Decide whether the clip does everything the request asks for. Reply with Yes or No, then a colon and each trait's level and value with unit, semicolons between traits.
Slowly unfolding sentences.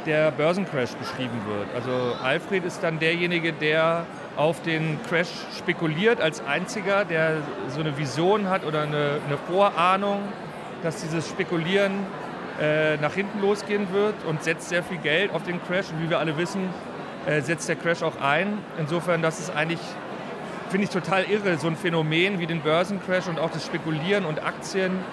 No: average, 175 wpm